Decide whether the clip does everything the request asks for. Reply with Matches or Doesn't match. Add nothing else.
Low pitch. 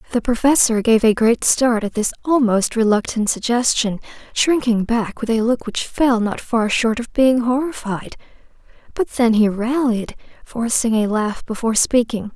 Doesn't match